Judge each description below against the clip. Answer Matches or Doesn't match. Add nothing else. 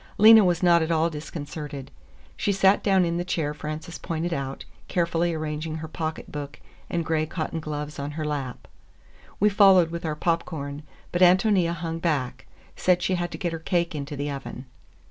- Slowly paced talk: Doesn't match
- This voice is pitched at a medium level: Matches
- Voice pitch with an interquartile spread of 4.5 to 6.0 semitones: Doesn't match